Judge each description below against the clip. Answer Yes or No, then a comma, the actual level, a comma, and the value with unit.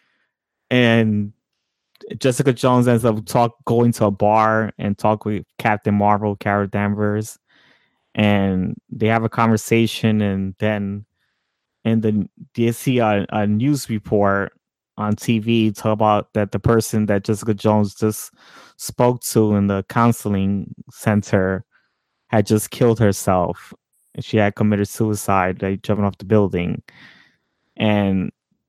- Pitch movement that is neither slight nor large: No, narrow, 2.0 semitones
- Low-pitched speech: Yes, low, 105 Hz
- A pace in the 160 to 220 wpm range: No, slow, 135 wpm